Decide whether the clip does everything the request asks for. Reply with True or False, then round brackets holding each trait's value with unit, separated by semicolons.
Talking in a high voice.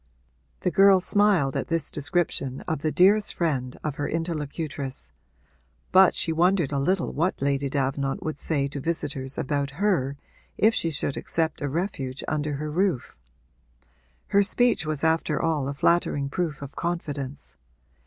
False (155 Hz)